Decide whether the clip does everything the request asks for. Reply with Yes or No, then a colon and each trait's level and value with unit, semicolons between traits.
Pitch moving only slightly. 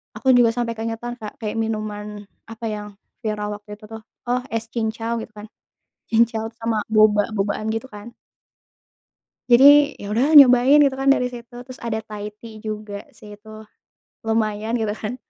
Yes: narrow, 2.2 semitones